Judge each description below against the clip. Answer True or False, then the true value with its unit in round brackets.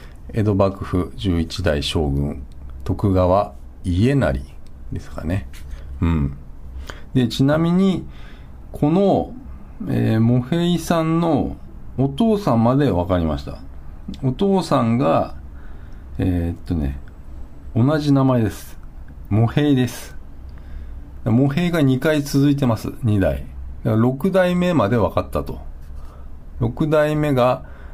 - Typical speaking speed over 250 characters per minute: False (185 characters per minute)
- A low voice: True (90 Hz)